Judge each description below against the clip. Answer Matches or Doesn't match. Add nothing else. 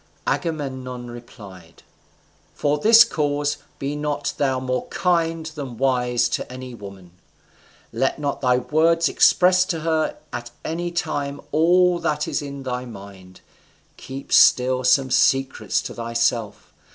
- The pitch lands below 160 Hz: Matches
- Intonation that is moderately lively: Matches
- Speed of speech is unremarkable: Doesn't match